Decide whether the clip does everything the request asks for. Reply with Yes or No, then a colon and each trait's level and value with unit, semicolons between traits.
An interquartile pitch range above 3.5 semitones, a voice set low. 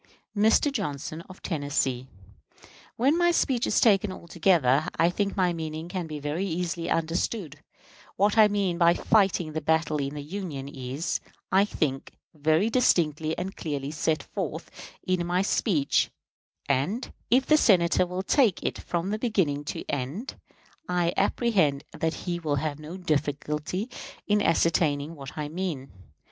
No: average, 4.6 semitones; medium, 170 Hz